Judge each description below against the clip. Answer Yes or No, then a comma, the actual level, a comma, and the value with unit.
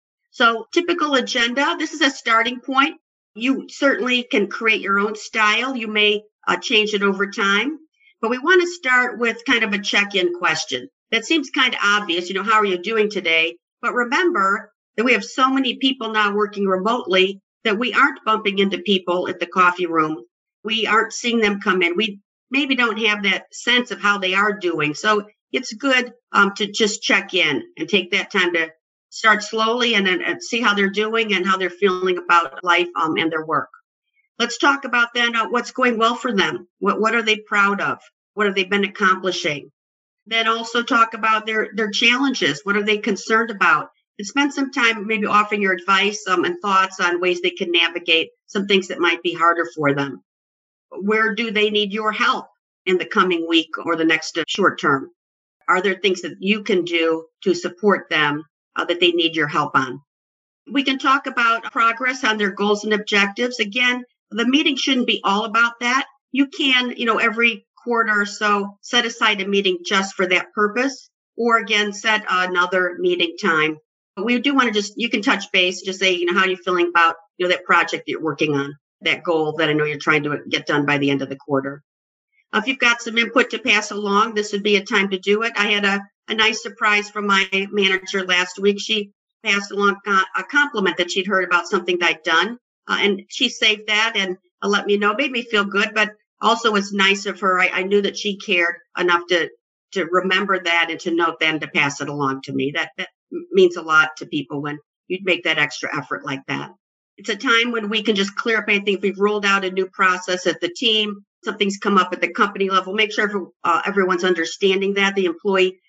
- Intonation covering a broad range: No, average, 4.1 semitones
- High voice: Yes, high, 205 Hz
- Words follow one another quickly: Yes, fast, 215 wpm